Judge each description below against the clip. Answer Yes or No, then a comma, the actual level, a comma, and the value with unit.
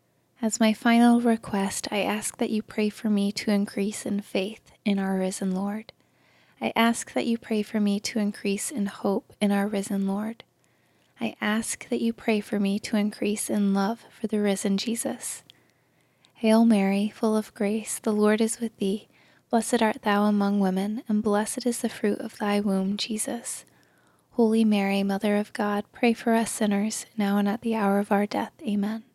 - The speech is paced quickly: No, average, 185 wpm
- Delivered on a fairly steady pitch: Yes, narrow, 1.9 semitones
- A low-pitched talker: No, high, 210 Hz